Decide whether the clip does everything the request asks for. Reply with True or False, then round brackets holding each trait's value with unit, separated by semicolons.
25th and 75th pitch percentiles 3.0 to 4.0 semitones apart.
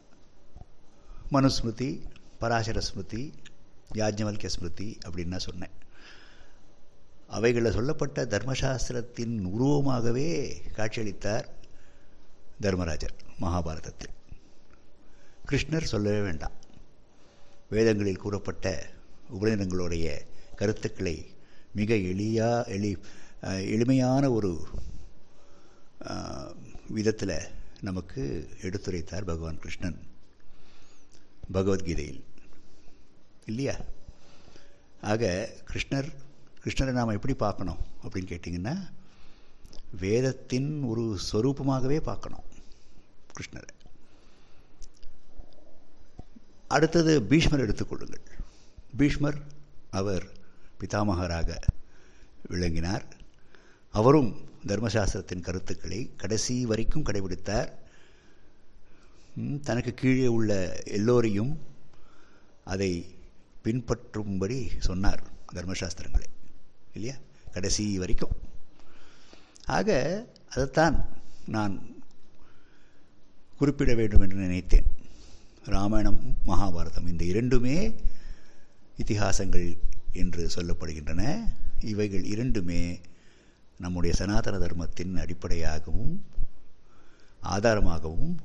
False (4.6 semitones)